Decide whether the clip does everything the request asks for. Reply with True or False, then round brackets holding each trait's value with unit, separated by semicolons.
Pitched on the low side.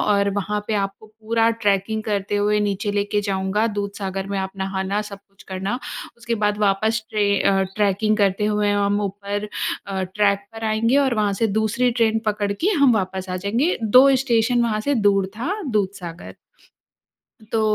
False (205 Hz)